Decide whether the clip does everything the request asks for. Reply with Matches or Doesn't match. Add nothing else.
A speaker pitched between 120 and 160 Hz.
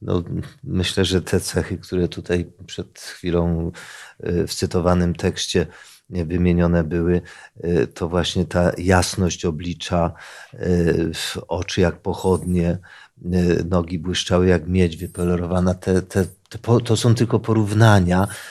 Doesn't match